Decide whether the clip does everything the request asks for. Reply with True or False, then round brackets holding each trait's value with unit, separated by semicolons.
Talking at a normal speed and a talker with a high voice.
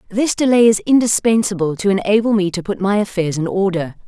True (190 wpm; 200 Hz)